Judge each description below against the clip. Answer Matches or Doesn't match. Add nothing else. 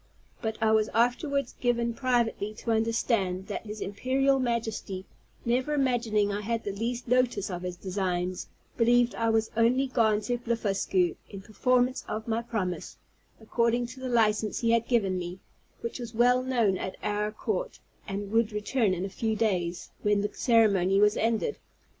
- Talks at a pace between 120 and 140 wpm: Doesn't match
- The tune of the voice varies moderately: Matches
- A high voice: Matches